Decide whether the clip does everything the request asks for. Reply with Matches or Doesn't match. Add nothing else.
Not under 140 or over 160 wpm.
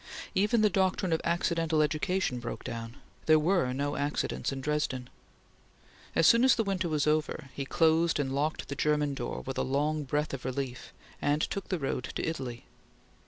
Doesn't match